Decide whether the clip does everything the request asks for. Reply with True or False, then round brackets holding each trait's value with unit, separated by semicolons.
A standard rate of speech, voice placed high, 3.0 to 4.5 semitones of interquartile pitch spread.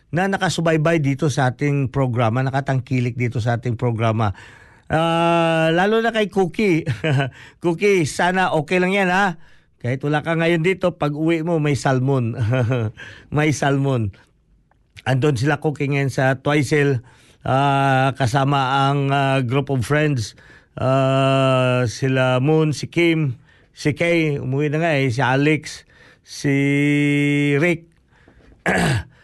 False (125 wpm; 140 Hz; 3.7 semitones)